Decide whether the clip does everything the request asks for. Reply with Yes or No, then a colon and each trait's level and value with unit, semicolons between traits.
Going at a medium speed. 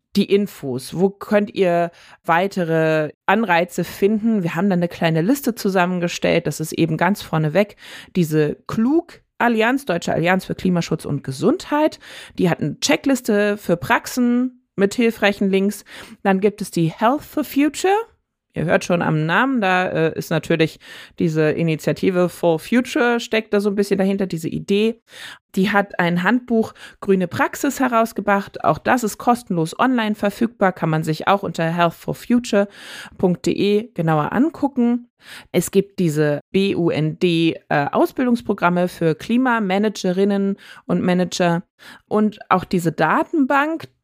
Yes: average, 135 wpm